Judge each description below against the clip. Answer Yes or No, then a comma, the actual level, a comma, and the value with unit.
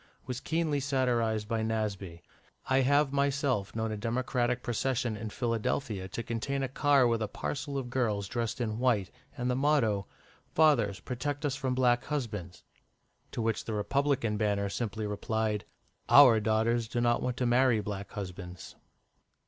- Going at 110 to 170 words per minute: Yes, average, 155 wpm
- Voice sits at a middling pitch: No, low, 120 Hz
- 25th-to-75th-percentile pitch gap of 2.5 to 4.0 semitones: Yes, average, 3.6 semitones